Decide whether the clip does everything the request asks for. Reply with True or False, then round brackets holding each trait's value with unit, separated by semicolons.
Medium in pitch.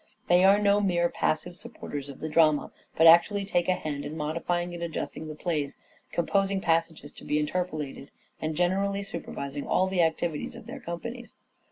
True (170 Hz)